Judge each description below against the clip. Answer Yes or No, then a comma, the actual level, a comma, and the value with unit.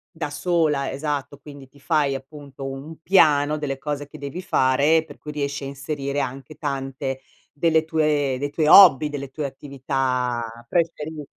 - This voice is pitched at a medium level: Yes, medium, 145 Hz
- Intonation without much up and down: Yes, narrow, 2.1 semitones